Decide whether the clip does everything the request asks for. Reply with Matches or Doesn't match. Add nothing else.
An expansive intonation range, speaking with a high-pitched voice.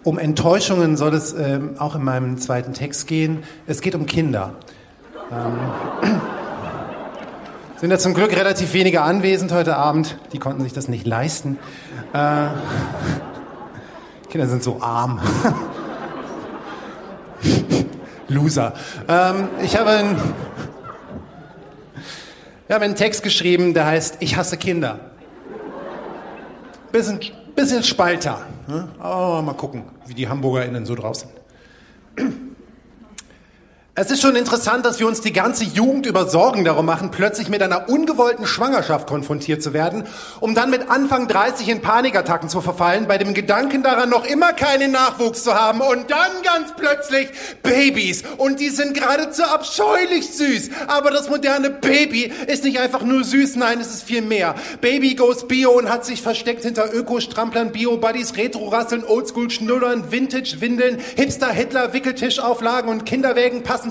Matches